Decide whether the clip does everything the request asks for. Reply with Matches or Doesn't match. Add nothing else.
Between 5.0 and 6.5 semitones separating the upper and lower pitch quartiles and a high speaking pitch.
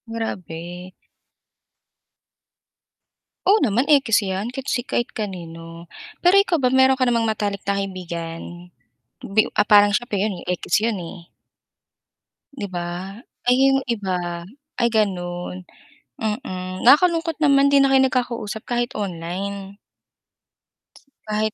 Matches